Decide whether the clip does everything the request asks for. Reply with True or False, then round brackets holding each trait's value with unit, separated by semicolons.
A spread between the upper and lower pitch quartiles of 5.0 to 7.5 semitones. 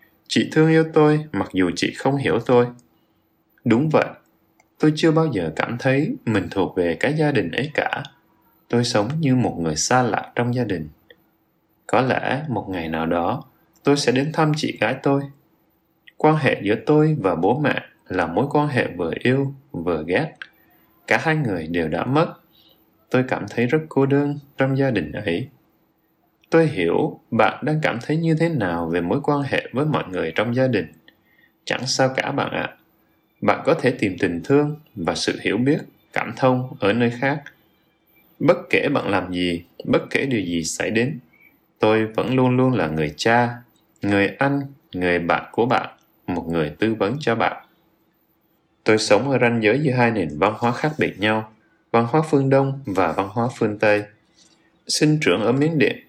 True (5.4 semitones)